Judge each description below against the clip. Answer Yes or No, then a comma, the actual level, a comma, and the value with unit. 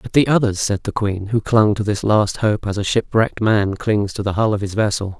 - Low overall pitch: Yes, low, 105 Hz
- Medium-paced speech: No, fast, 265 wpm